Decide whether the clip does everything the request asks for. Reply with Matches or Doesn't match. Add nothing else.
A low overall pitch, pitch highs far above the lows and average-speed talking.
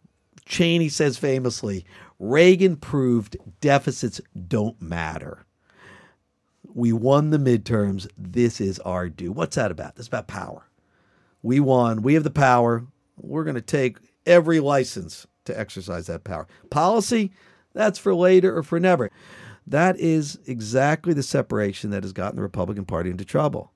Matches